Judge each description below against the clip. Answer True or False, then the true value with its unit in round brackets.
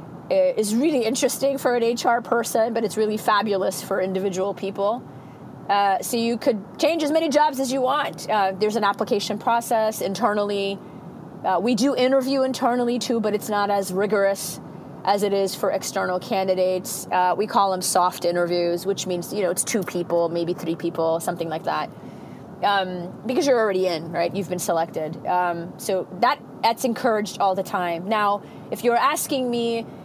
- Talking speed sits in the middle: False (180 wpm)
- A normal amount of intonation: True (4.3 semitones)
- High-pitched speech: True (205 Hz)